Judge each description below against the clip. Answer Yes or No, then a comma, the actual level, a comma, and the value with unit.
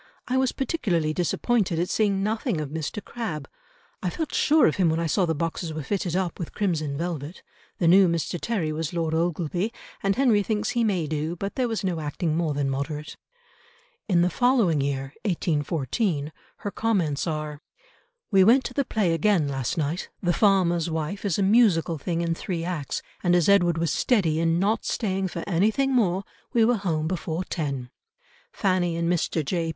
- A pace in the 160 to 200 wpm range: Yes, average, 190 wpm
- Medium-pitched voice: Yes, medium, 175 Hz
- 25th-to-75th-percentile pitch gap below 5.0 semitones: Yes, average, 4.1 semitones